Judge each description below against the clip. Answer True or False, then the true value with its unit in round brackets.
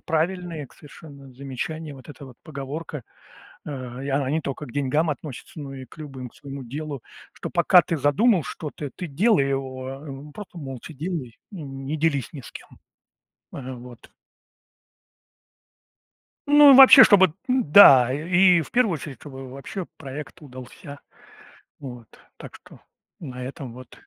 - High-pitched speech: False (145 Hz)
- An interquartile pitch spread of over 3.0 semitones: True (3.6 semitones)